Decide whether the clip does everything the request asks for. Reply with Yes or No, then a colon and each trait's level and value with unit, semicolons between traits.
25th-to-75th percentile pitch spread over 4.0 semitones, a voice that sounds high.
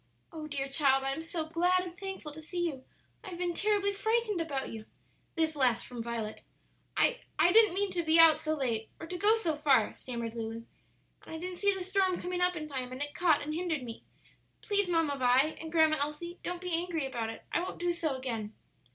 Yes: average, 4.9 semitones; very high, 320 Hz